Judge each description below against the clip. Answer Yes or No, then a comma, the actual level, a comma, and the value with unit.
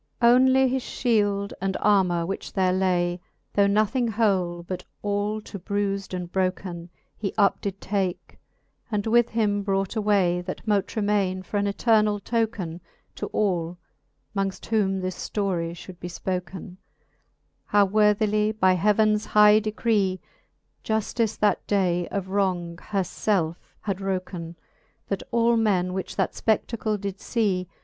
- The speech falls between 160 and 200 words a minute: No, average, 140 wpm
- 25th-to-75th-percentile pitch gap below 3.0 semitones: Yes, narrow, 2.5 semitones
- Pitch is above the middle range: Yes, high, 200 Hz